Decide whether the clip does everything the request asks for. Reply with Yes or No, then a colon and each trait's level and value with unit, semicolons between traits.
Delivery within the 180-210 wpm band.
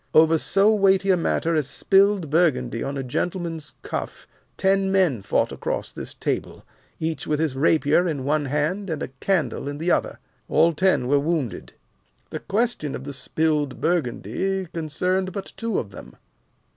No: average, 165 wpm